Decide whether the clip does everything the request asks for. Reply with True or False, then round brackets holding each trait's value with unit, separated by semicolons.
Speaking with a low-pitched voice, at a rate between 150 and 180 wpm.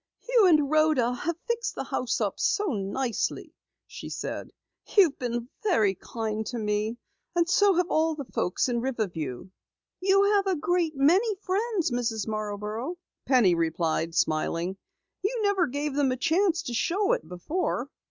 False (275 Hz; 155 wpm)